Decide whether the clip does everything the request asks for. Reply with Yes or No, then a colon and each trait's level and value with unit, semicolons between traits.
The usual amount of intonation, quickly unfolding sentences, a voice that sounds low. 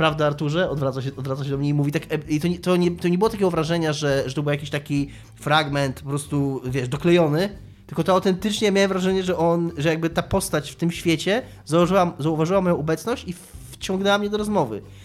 No: average, 4.0 semitones; fast, 220 wpm; medium, 160 Hz